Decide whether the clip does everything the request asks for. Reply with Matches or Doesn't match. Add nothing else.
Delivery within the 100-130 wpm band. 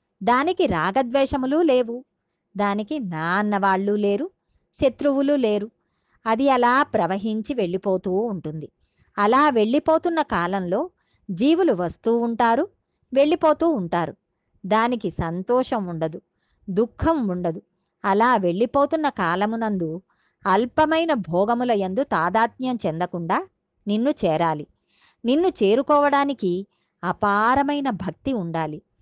Doesn't match